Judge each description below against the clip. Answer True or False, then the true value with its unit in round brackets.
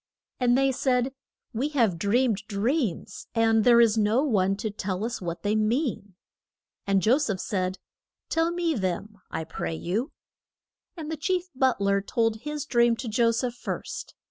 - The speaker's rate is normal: True (170 wpm)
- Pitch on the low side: False (230 Hz)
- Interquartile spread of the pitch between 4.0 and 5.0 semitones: True (4.6 semitones)